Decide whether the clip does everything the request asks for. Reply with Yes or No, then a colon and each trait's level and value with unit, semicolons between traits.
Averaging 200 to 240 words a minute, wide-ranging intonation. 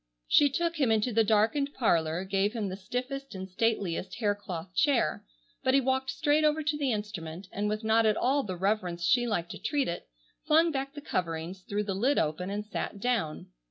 Yes: fast, 205 wpm; wide, 6.2 semitones